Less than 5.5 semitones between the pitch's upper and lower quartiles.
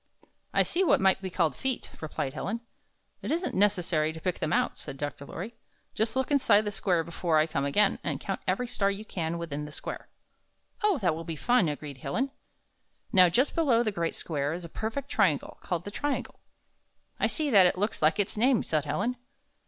No: wide, 6.5 semitones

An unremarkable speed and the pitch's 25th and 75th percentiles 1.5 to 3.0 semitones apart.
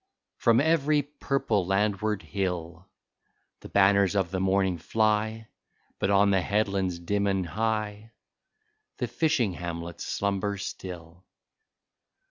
No: slow, 110 wpm; average, 2.7 semitones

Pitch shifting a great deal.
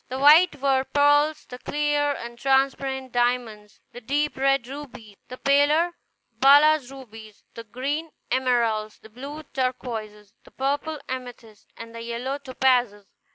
No: average, 3.4 semitones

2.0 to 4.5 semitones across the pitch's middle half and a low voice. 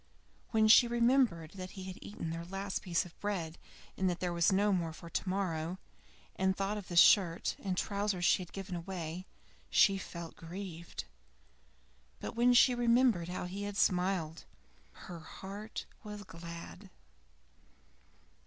No: average, 3.1 semitones; high, 190 Hz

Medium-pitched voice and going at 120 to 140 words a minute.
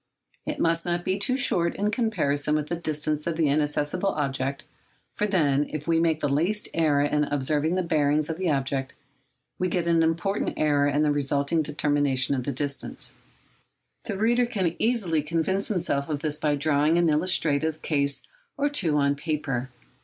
No: medium, 155 Hz; average, 175 wpm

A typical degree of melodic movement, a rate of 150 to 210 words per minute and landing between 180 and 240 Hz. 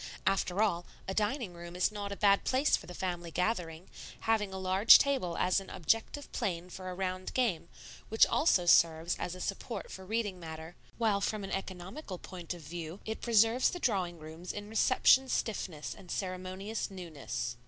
Yes: average, 3.5 semitones; average, 180 wpm; high, 190 Hz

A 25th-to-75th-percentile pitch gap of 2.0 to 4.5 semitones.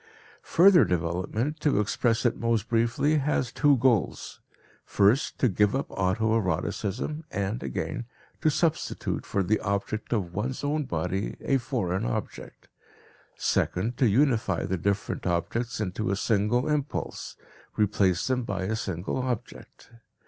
No: average, 4.9 semitones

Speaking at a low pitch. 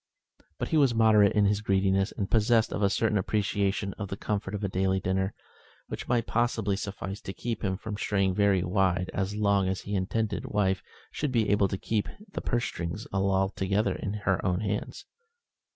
Yes: low, 100 Hz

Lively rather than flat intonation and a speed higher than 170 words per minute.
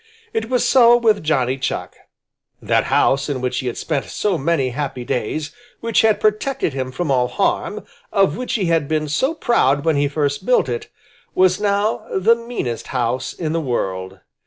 Yes: wide, 8.3 semitones; average, 180 wpm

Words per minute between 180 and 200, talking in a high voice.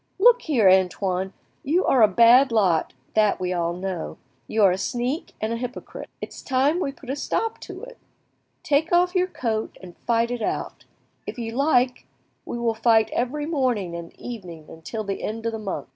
Yes: average, 190 wpm; high, 230 Hz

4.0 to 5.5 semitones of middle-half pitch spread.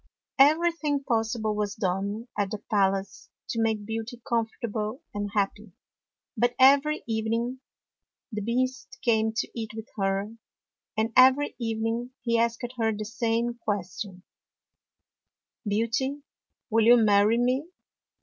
No: narrow, 2.5 semitones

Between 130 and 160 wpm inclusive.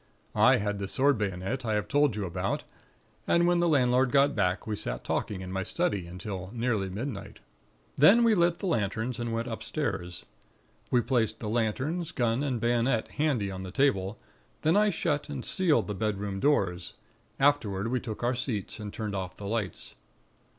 No: average, 180 wpm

